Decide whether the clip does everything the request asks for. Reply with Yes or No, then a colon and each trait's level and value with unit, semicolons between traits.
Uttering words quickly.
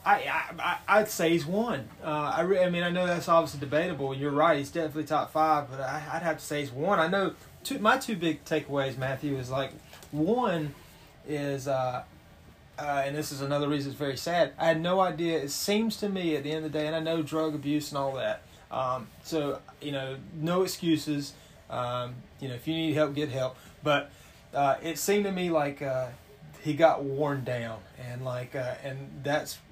Yes: fast, 215 wpm